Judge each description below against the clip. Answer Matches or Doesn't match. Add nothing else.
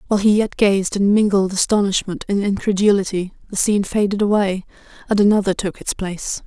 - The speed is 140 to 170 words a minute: Matches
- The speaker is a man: Doesn't match